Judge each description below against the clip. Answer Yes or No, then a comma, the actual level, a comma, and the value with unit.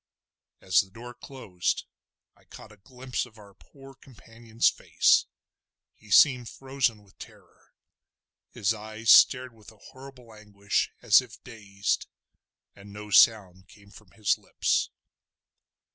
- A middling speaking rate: No, slow, 130 wpm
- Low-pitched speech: Yes, low, 110 Hz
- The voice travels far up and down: No, average, 3.5 semitones